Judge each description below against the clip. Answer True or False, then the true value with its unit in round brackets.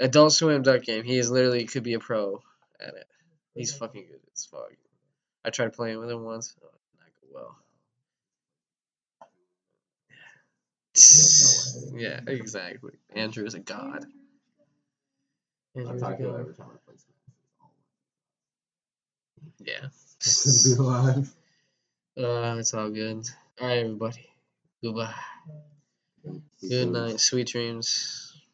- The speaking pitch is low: True (125 Hz)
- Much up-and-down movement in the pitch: False (3.9 semitones)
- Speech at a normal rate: False (105 wpm)